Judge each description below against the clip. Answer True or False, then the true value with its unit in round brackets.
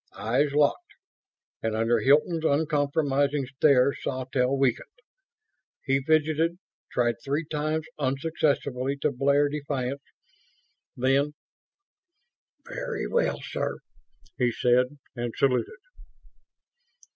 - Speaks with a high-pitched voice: False (140 Hz)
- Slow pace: True (90 wpm)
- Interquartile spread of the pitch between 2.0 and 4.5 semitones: True (2.9 semitones)